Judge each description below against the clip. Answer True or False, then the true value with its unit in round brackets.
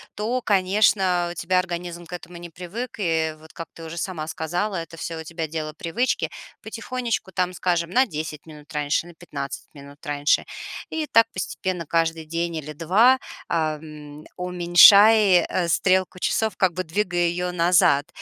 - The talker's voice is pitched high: False (175 Hz)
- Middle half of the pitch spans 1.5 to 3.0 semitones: True (2.7 semitones)